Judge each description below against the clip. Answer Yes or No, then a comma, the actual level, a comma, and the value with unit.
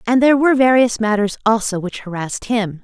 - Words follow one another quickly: No, average, 190 wpm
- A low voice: No, high, 220 Hz